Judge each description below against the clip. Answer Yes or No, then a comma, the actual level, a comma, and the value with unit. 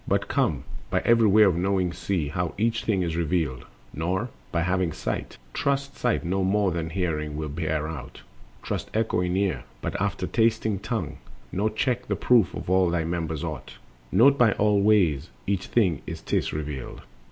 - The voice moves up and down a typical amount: Yes, average, 4.8 semitones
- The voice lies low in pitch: Yes, very low, 95 Hz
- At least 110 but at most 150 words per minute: No, average, 175 wpm